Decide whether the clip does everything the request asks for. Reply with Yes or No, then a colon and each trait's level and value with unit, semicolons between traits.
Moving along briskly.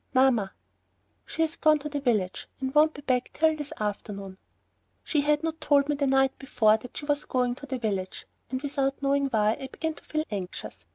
Yes: fast, 210 wpm